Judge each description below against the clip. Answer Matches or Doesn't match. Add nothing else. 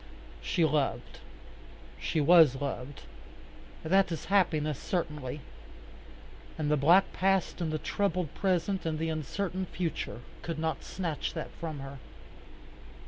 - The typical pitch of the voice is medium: Matches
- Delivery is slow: Matches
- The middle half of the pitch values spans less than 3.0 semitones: Doesn't match